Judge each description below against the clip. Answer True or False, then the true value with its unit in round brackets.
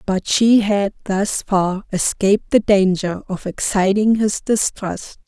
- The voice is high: True (200 Hz)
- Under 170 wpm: True (135 wpm)